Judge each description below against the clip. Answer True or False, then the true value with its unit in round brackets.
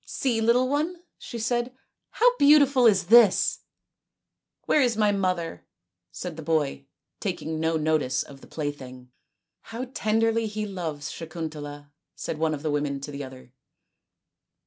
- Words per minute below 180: True (170 wpm)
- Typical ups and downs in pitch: False (7.8 semitones)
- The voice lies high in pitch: False (170 Hz)